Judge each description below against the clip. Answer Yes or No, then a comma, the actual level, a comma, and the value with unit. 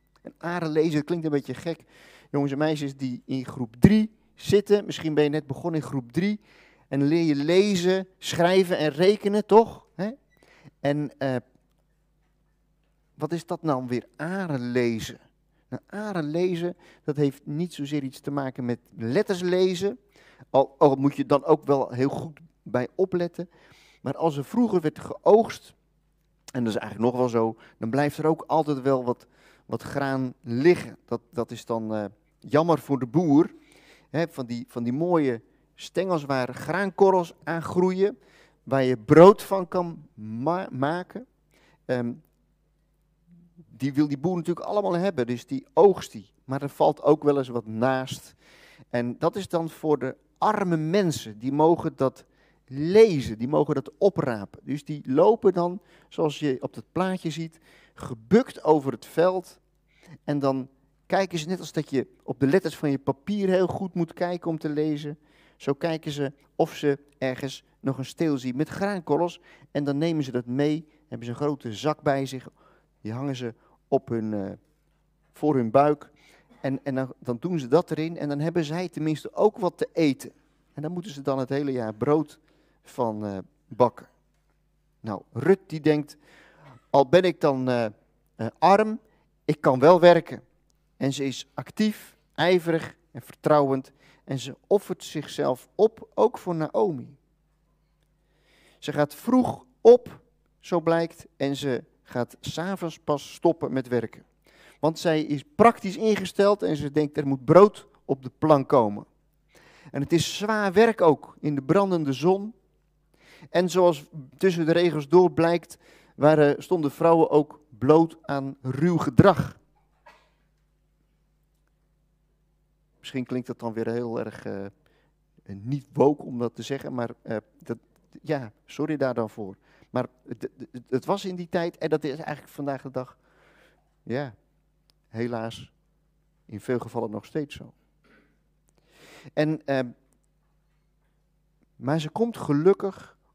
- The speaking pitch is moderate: Yes, medium, 150 Hz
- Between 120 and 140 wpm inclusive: No, average, 160 wpm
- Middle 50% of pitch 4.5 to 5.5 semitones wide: No, average, 4.0 semitones